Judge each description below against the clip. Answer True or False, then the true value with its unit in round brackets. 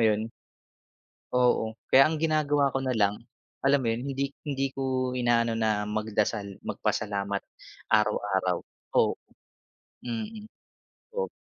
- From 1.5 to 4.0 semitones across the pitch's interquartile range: False (4.4 semitones)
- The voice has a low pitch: True (120 Hz)